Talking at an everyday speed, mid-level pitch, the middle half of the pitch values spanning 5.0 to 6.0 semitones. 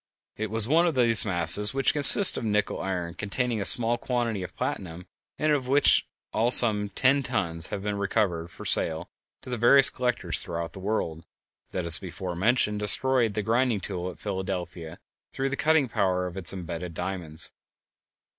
No: average, 180 wpm; low, 105 Hz; wide, 5.5 semitones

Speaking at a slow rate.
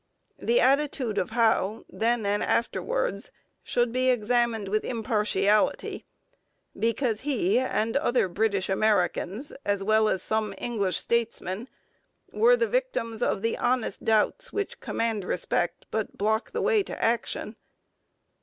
Yes: slow, 130 wpm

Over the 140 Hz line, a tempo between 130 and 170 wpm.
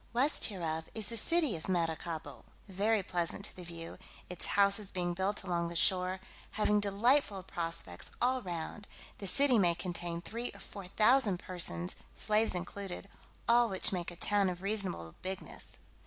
Yes: high, 190 Hz; average, 160 wpm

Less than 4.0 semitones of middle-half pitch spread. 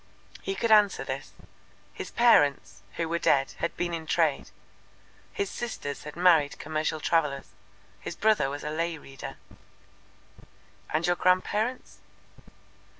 No: average, 4.6 semitones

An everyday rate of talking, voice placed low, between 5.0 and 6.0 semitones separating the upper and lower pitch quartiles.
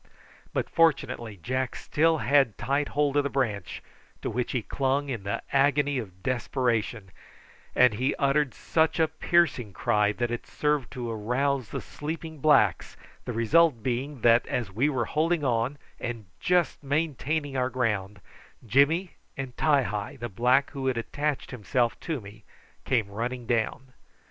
No: average, 155 wpm; low, 130 Hz; average, 4.0 semitones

